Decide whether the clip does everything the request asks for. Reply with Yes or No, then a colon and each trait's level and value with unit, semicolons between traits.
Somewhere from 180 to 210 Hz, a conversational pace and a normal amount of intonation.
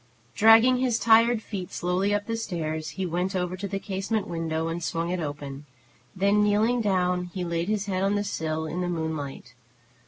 Yes: medium, 185 Hz; average, 190 wpm; average, 3.8 semitones